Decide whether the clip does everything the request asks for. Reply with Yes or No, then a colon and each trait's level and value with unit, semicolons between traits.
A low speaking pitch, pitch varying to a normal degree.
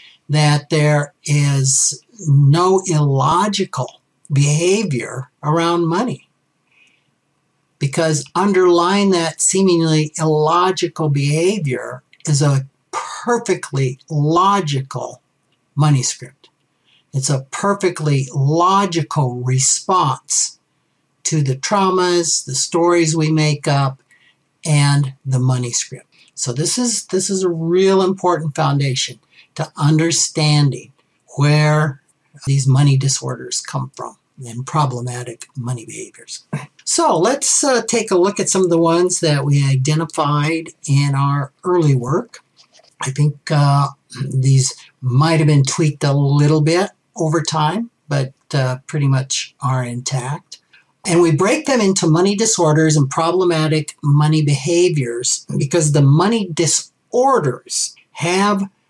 No: medium, 155 Hz; average, 3.7 semitones